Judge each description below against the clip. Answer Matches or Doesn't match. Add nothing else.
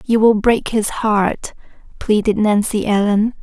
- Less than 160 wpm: Matches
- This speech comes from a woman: Matches